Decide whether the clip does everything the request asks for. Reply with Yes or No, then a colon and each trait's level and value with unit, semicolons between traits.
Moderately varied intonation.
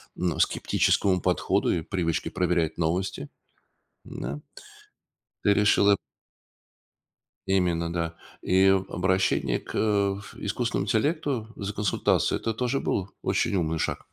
Yes: average, 3.5 semitones